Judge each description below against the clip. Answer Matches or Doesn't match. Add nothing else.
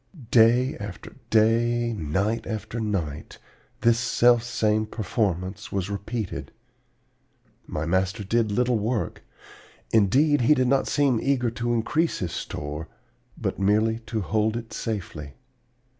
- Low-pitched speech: Matches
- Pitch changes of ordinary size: Matches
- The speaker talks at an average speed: Doesn't match